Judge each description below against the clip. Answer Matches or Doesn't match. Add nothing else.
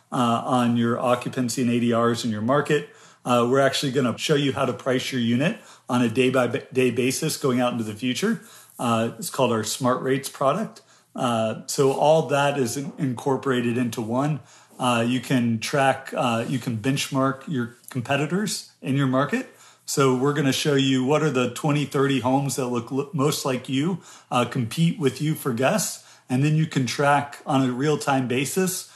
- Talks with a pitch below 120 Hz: Doesn't match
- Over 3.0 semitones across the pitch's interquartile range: Doesn't match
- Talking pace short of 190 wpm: Doesn't match